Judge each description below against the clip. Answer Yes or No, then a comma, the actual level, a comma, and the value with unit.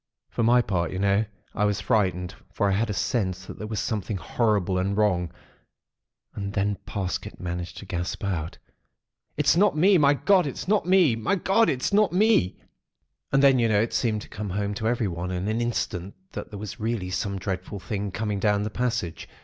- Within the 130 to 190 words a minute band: No, average, 200 wpm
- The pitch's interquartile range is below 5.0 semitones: Yes, average, 4.0 semitones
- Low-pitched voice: Yes, low, 105 Hz